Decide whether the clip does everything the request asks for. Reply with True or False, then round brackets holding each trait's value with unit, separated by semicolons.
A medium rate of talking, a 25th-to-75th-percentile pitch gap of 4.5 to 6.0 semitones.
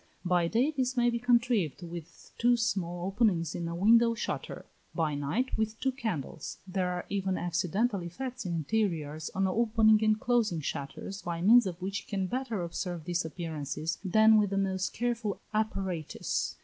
True (170 wpm; 4.9 semitones)